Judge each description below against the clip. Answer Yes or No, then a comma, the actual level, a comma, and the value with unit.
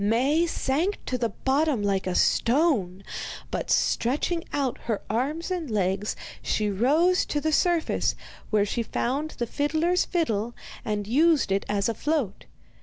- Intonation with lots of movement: Yes, wide, 7.0 semitones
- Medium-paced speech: Yes, average, 150 wpm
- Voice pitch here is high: Yes, very high, 260 Hz